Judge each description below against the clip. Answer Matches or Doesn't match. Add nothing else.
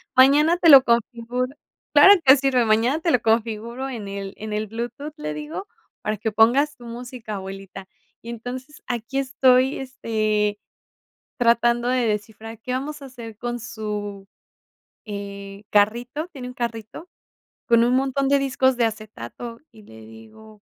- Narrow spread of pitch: Doesn't match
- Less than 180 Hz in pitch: Doesn't match